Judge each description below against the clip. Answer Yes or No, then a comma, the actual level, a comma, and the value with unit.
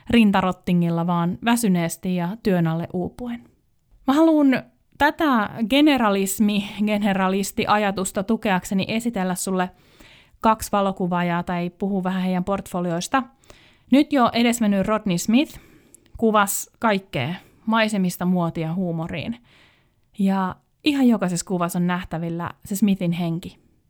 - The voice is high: Yes, high, 195 Hz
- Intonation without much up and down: No, average, 3.9 semitones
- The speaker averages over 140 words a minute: No, average, 105 wpm